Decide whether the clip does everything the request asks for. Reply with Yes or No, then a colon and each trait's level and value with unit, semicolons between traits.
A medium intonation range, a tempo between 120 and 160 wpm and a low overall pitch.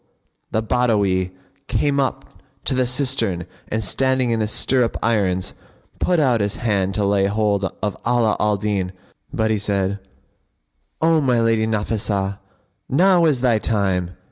Yes: average, 3.9 semitones; average, 145 wpm; low, 110 Hz